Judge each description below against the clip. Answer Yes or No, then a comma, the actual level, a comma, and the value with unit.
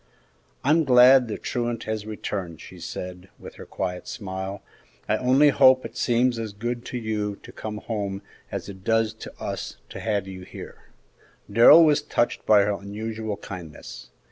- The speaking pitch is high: No, low, 110 Hz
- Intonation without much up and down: No, average, 3.5 semitones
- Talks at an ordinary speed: Yes, average, 170 wpm